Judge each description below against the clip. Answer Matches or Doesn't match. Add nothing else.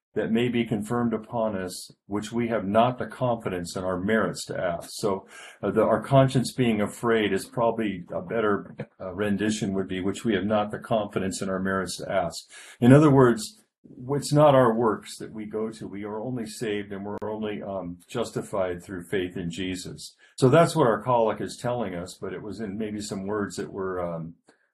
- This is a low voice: Matches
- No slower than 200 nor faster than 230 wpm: Matches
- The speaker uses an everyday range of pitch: Matches